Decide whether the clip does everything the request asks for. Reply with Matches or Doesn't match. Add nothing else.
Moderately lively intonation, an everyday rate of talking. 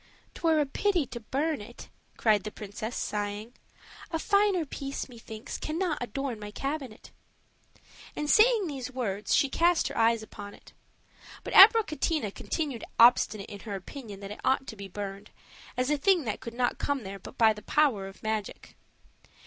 Doesn't match